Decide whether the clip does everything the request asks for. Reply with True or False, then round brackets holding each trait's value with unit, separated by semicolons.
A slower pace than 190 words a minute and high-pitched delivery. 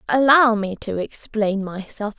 True (135 wpm; 220 Hz)